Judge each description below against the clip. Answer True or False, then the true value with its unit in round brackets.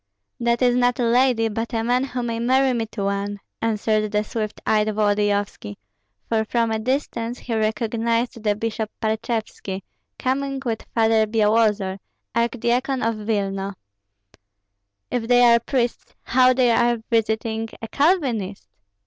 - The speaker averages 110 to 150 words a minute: True (140 wpm)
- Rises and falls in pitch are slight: True (2.2 semitones)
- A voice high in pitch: True (225 Hz)